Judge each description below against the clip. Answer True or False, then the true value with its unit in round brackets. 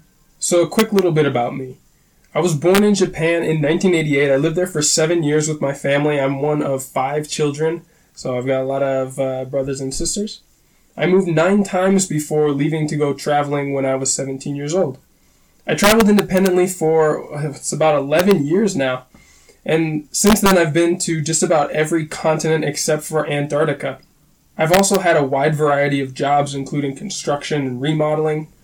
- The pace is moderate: True (180 wpm)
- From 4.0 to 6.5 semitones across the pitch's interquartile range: False (3.3 semitones)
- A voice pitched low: False (155 Hz)